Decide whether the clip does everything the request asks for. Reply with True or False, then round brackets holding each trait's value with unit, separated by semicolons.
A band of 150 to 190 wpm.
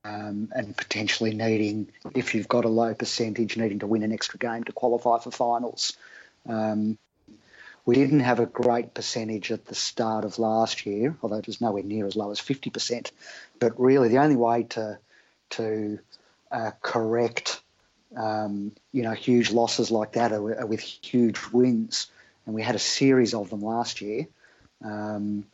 True (170 wpm)